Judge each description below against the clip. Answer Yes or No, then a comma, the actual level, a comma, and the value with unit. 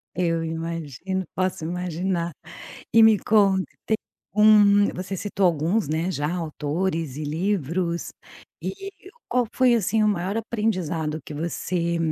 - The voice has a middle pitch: Yes, medium, 180 Hz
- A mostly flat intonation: No, average, 3.8 semitones